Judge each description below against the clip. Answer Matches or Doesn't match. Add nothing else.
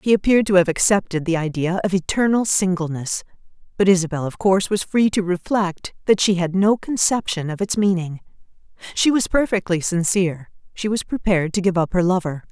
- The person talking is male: Doesn't match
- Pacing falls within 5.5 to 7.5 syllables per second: Matches